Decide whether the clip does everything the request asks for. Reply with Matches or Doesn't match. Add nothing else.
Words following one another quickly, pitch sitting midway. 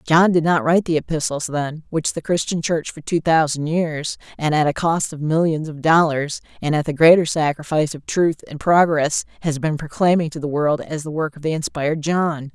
Matches